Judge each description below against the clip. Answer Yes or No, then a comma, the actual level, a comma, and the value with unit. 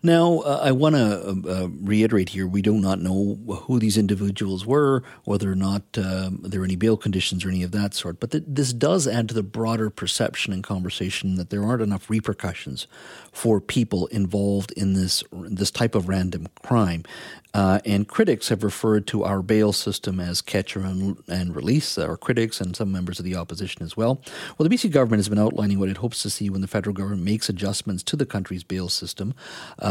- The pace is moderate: No, fast, 215 wpm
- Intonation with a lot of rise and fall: No, average, 2.9 semitones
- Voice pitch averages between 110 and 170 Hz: No, low, 100 Hz